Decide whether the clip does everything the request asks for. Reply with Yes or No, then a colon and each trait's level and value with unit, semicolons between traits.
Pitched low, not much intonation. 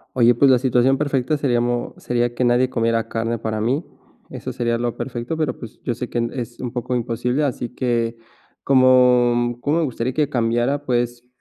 Yes: low, 120 Hz; narrow, 1.5 semitones